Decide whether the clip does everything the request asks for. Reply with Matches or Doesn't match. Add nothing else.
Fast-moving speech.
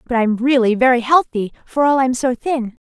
Matches